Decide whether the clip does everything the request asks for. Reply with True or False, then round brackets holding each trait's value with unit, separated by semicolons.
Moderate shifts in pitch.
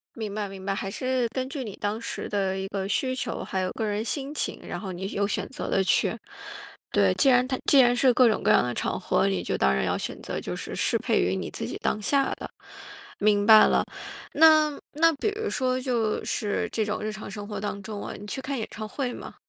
True (4.7 semitones)